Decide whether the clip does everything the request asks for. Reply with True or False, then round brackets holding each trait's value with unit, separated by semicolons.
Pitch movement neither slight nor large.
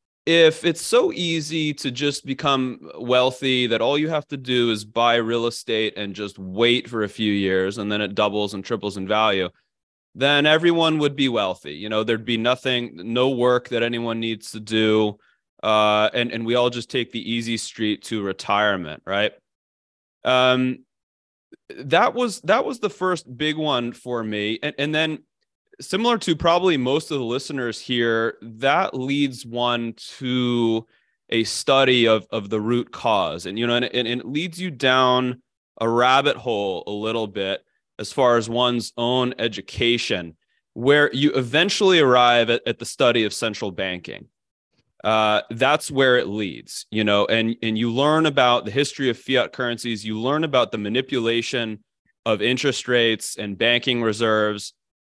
True (3.5 semitones)